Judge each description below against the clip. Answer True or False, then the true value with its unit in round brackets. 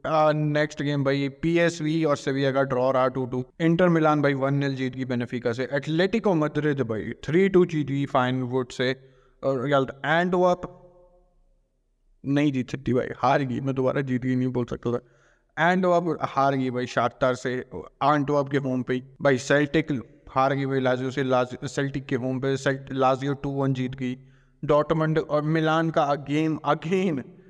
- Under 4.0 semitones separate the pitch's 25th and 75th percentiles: True (2.8 semitones)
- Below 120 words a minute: True (110 wpm)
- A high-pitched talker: False (140 Hz)